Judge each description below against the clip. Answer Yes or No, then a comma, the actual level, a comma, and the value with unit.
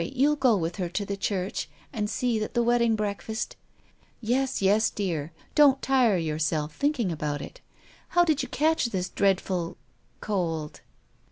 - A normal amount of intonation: No, wide, 6.3 semitones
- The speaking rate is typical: Yes, average, 170 wpm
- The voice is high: Yes, high, 210 Hz